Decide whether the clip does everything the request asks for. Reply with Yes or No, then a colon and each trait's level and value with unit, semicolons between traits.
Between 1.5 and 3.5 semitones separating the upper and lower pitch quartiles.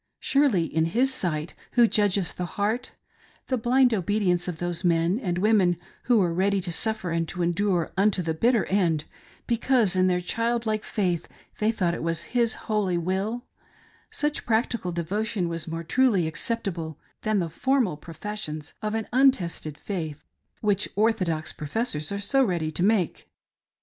No: average, 4.7 semitones